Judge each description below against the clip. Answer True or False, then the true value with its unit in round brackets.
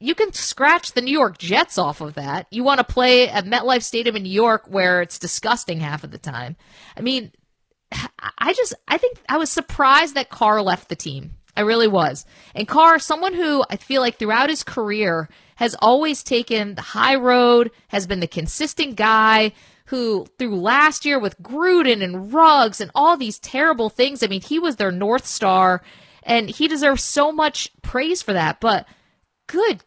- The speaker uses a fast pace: False (190 wpm)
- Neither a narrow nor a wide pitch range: False (6.3 semitones)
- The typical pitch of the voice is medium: False (235 Hz)